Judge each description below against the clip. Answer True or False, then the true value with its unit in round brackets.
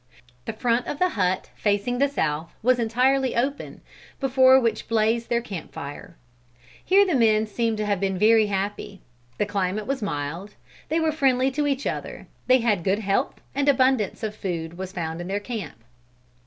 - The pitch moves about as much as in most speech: True (4.9 semitones)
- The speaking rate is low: False (180 wpm)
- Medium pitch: False (220 Hz)